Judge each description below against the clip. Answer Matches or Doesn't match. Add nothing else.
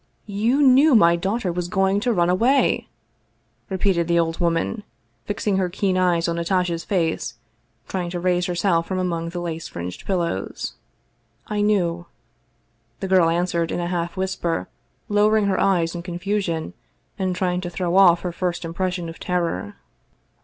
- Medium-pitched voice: Matches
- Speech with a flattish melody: Matches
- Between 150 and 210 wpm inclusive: Matches